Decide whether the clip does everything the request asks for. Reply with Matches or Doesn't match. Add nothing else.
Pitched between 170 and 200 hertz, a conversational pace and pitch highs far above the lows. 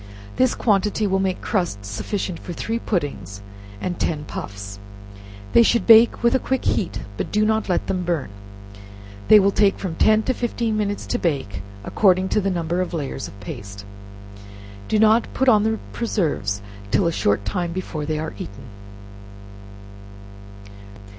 Matches